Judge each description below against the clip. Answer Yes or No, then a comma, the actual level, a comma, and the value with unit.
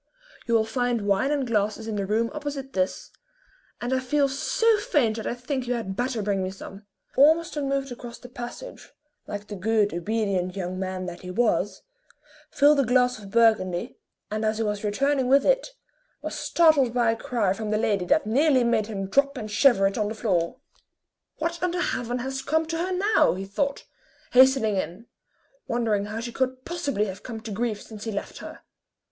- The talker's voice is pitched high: Yes, high, 230 Hz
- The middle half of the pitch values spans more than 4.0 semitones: Yes, average, 4.8 semitones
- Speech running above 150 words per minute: Yes, average, 195 wpm